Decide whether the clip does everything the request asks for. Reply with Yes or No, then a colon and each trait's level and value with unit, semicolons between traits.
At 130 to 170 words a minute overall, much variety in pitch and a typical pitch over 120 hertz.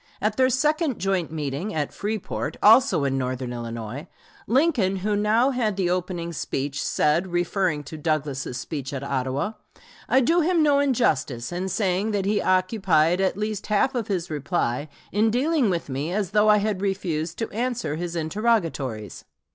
Yes: average, 165 wpm; wide, 6.3 semitones; medium, 185 Hz